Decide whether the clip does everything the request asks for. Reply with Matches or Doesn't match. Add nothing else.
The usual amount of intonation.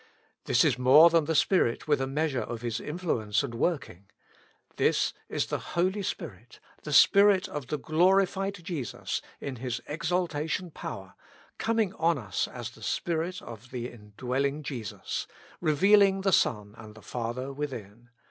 Doesn't match